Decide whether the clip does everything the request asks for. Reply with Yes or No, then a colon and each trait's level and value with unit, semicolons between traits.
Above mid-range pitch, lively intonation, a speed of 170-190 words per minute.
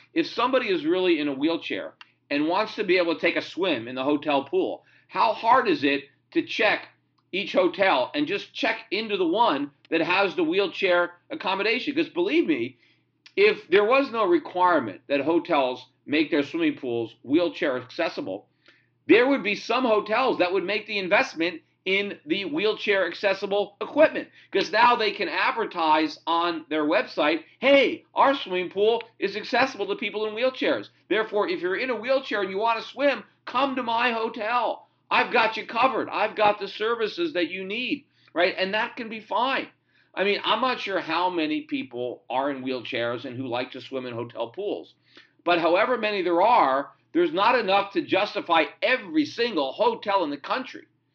Yes: high, 215 Hz; wide, 8.9 semitones; average, 180 wpm